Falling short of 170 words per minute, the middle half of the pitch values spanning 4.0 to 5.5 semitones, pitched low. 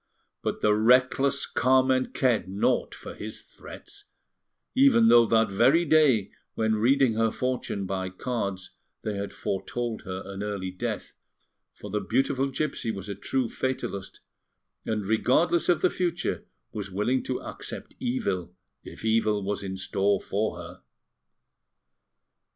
Yes: average, 140 wpm; average, 4.7 semitones; low, 110 Hz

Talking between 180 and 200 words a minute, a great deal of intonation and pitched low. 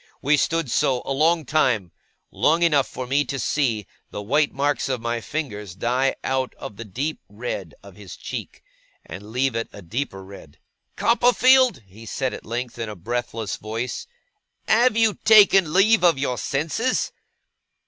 No: average, 165 wpm; wide, 5.9 semitones; low, 130 Hz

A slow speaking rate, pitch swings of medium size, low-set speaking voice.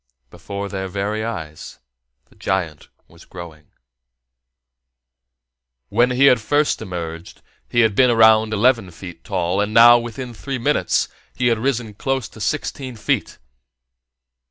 Yes: slow, 130 wpm; average, 4.3 semitones; low, 110 Hz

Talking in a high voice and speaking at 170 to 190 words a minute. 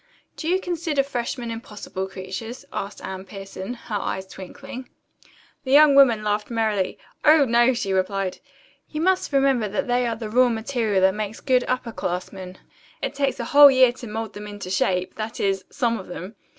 Yes: high, 225 Hz; average, 180 wpm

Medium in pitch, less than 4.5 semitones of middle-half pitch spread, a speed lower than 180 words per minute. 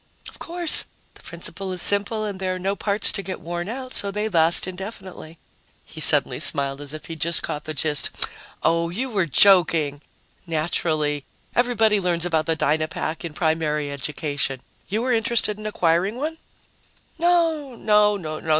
No: medium, 180 Hz; average, 5.1 semitones; average, 160 wpm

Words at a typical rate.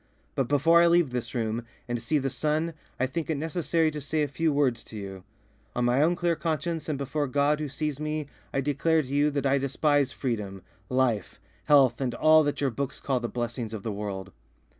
No: fast, 215 wpm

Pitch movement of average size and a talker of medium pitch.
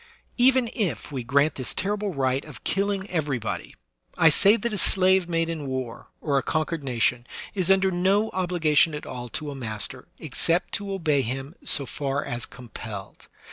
No: wide, 6.2 semitones; medium, 155 Hz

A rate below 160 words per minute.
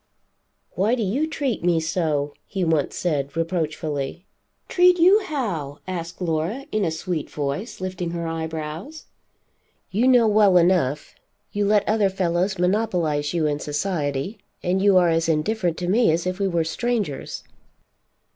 Yes: average, 150 wpm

